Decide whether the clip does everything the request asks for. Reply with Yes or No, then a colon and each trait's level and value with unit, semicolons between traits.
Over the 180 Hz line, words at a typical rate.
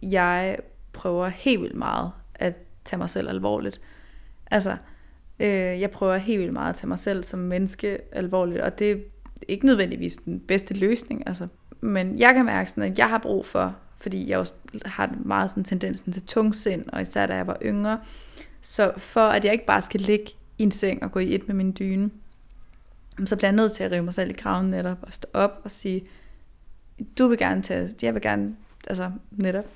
Yes: high, 190 Hz; average, 210 wpm